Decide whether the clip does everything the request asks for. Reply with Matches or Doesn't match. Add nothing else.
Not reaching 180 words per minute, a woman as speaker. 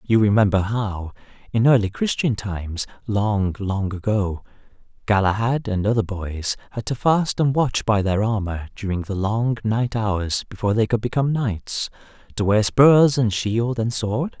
Doesn't match